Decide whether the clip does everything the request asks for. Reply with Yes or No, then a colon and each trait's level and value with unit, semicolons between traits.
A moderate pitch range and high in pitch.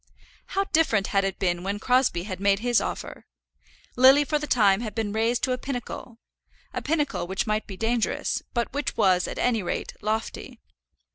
Yes: average, 4.2 semitones; high, 225 Hz